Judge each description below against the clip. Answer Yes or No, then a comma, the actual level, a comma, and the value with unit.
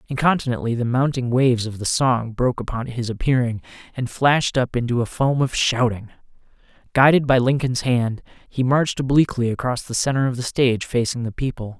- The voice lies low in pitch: Yes, low, 125 Hz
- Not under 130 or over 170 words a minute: No, average, 180 wpm